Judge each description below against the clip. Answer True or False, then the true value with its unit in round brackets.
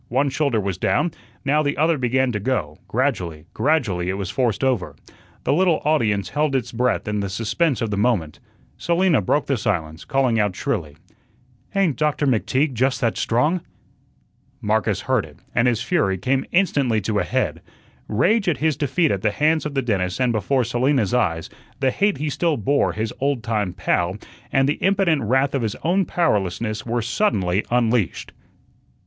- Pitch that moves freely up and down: True (5.9 semitones)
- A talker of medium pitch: False (125 Hz)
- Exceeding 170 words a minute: True (180 wpm)